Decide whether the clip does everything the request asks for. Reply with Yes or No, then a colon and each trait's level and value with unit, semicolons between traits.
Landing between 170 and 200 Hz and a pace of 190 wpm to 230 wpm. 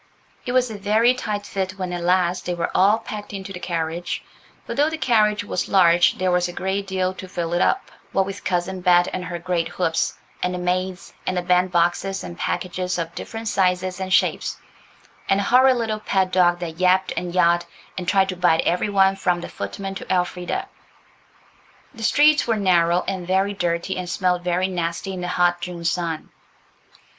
Yes: medium, 185 Hz; average, 200 wpm